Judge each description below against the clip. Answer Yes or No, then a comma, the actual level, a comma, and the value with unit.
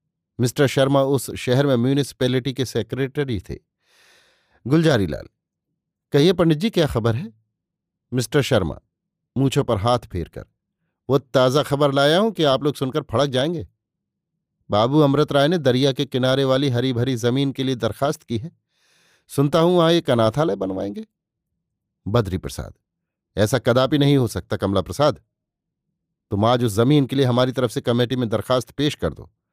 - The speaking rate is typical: Yes, average, 160 wpm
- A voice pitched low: Yes, low, 130 Hz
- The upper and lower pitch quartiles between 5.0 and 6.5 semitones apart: No, average, 3.7 semitones